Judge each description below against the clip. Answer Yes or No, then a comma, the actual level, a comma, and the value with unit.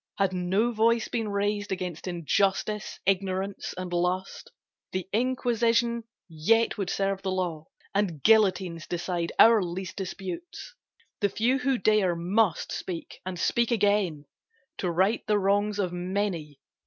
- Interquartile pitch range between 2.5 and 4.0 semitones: Yes, average, 3.1 semitones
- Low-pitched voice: No, high, 195 Hz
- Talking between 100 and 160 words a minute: Yes, slow, 135 wpm